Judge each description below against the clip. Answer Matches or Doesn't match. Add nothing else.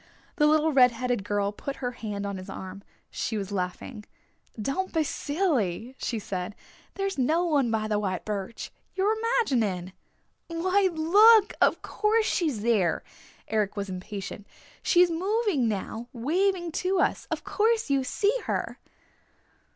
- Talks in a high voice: Matches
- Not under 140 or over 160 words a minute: Matches